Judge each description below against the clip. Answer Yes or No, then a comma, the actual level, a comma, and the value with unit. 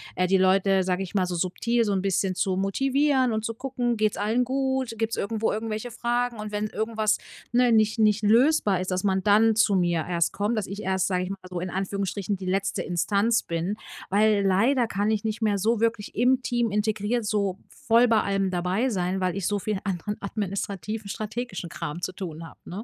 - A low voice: No, high, 205 Hz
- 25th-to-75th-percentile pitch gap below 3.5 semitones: Yes, average, 3.1 semitones